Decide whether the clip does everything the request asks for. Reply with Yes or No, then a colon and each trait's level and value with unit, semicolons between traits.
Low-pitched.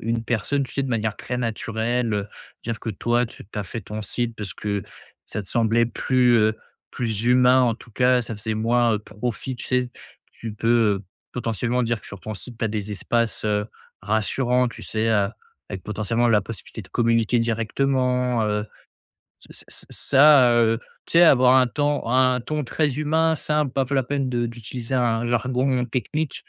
Yes: low, 120 Hz